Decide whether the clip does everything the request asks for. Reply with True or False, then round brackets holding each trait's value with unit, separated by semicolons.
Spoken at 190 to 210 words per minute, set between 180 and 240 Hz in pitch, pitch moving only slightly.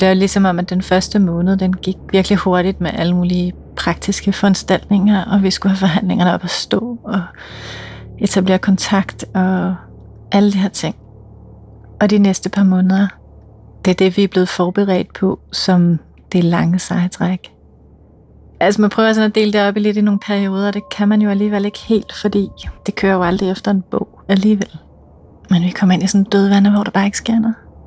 True (200 wpm; 190 Hz; 2.2 semitones)